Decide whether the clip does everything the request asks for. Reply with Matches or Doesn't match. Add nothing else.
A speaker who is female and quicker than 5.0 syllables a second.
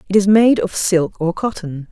Doesn't match